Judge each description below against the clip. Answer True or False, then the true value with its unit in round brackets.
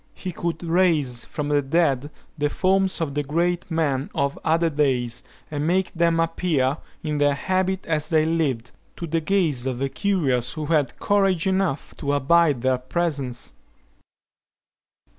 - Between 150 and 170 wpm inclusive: True (155 wpm)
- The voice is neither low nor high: True (155 Hz)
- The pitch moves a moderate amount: True (3.7 semitones)